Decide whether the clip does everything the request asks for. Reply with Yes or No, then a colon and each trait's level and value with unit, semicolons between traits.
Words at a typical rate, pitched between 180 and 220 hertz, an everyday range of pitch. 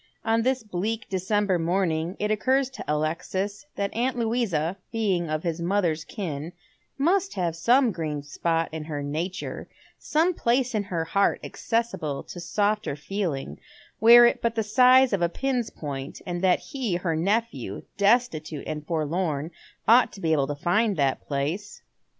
No: average, 160 wpm; high, 190 Hz; wide, 6.2 semitones